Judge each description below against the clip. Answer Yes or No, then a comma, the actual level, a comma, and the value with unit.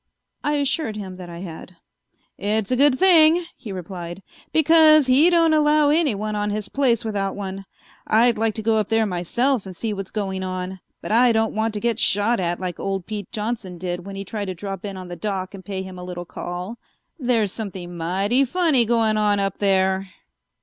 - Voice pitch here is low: No, high, 205 Hz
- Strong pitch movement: No, average, 4.1 semitones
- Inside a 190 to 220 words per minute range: Yes, fast, 205 wpm